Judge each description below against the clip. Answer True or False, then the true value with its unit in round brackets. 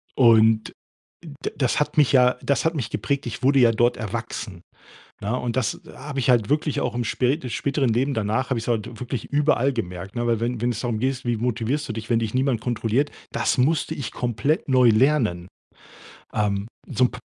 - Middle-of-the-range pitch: False (120 Hz)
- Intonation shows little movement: False (3.2 semitones)